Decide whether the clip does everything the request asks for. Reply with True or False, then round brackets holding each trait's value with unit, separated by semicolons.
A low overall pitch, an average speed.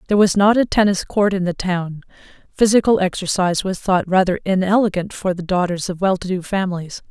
False (190 Hz; 195 wpm)